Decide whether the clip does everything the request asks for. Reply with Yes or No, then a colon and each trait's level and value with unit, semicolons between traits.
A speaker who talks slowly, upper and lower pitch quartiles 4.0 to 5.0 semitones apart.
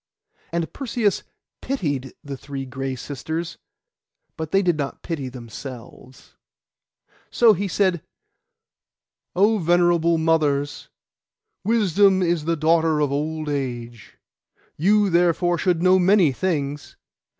Yes: slow, 110 wpm; average, 4.4 semitones